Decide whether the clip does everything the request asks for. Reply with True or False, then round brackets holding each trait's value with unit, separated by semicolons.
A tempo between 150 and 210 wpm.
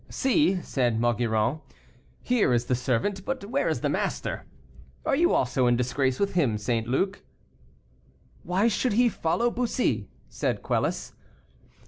False (140 wpm)